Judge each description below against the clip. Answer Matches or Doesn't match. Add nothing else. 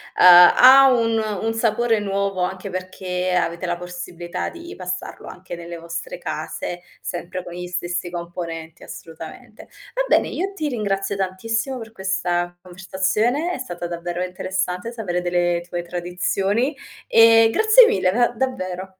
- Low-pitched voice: Doesn't match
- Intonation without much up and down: Doesn't match